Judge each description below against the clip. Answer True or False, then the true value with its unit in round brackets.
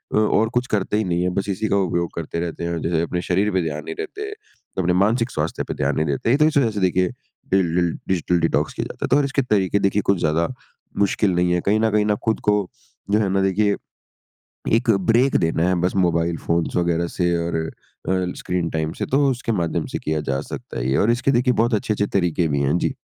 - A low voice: True (95 Hz)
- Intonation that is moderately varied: True (4.2 semitones)